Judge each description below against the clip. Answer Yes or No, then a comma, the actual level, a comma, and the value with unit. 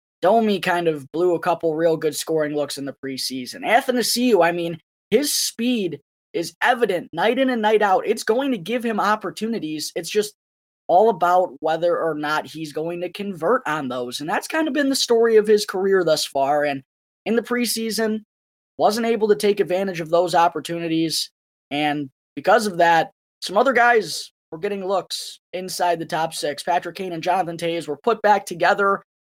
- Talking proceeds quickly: No, average, 185 wpm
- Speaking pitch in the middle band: Yes, medium, 180 Hz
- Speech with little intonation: No, average, 5.2 semitones